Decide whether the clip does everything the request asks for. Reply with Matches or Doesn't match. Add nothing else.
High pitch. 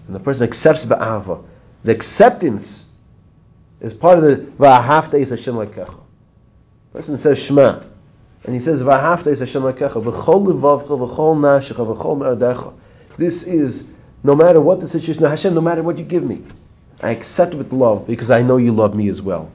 Doesn't match